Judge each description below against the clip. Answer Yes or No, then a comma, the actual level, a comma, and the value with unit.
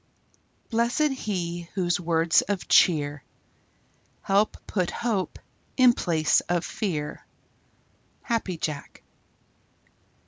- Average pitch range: Yes, average, 4.8 semitones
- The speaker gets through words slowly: Yes, slow, 90 wpm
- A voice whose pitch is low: No, medium, 180 Hz